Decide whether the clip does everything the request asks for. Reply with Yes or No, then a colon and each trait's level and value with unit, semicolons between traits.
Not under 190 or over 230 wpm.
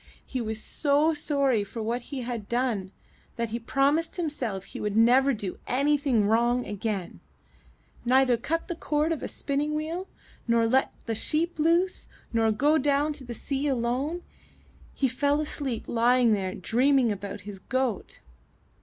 No: average, 165 wpm